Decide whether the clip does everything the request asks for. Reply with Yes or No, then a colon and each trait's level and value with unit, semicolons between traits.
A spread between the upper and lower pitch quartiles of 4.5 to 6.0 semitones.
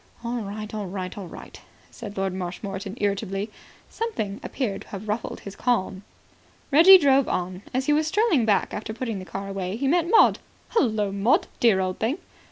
Yes: average, 4.8 semitones